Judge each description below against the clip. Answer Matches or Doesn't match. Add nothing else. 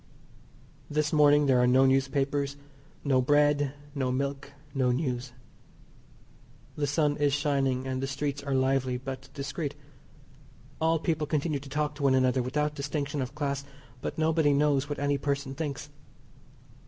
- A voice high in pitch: Doesn't match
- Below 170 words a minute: Matches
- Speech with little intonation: Matches